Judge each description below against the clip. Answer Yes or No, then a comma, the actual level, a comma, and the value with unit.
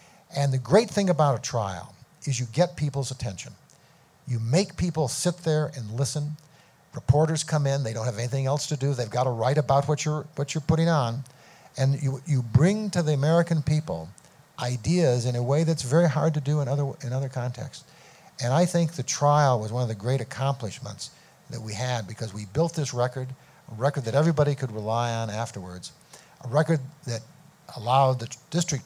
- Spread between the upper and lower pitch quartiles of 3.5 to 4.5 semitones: Yes, average, 3.8 semitones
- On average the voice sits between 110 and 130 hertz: No, medium, 140 Hz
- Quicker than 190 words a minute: Yes, average, 200 wpm